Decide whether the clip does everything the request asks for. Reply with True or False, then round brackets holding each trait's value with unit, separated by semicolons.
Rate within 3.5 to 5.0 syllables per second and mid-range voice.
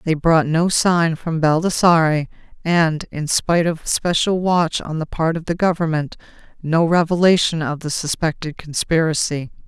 True (4.5 syllables/s; 160 Hz)